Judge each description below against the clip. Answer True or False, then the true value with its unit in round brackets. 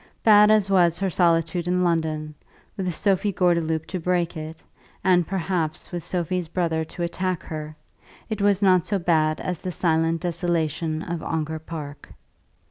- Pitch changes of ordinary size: False (2.3 semitones)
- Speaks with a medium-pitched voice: True (170 Hz)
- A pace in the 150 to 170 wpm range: True (155 wpm)